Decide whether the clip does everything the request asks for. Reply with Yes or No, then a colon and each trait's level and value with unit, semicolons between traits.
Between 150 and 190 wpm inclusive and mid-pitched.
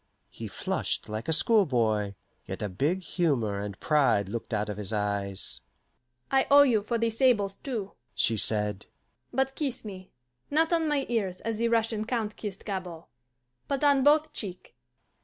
No: average, 165 wpm; high, 195 Hz